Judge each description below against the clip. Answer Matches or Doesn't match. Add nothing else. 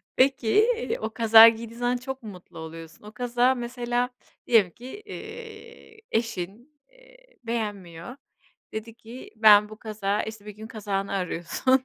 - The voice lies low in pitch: Doesn't match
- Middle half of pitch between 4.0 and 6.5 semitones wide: Doesn't match